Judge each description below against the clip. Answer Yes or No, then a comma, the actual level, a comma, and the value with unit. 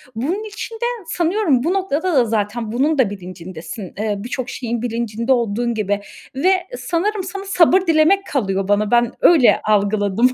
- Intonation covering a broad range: Yes, wide, 8.7 semitones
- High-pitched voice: Yes, high, 240 Hz